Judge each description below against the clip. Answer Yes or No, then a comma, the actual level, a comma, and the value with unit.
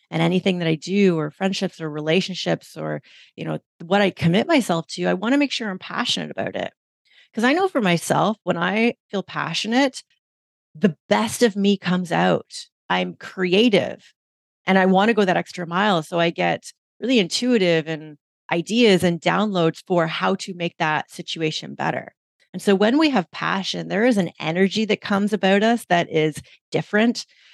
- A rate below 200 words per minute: Yes, average, 185 wpm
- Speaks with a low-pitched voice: No, medium, 185 Hz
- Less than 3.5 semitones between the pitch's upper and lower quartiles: No, average, 4.1 semitones